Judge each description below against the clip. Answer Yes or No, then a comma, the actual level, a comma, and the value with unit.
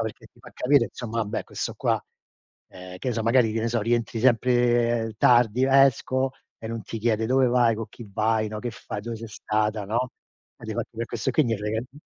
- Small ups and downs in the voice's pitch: Yes, narrow, 2.0 semitones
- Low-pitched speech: Yes, low, 115 Hz